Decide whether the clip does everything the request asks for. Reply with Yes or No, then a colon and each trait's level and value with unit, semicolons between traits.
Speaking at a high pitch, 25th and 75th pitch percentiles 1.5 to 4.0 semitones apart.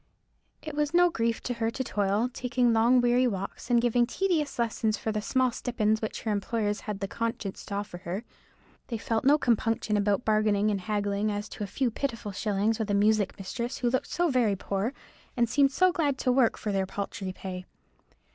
Yes: high, 225 Hz; average, 3.3 semitones